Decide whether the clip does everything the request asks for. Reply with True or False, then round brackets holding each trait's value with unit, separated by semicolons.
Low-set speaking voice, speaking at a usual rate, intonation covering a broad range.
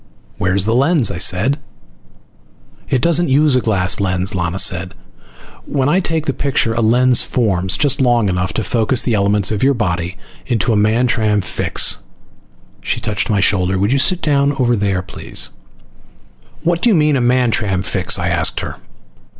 True (110 Hz; 175 wpm; 5.7 semitones)